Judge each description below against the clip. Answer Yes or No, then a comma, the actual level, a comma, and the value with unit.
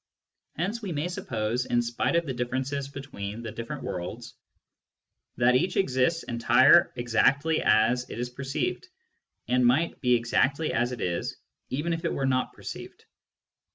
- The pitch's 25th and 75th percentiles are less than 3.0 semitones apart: No, average, 3.3 semitones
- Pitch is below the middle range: Yes, low, 125 Hz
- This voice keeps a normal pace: Yes, average, 155 wpm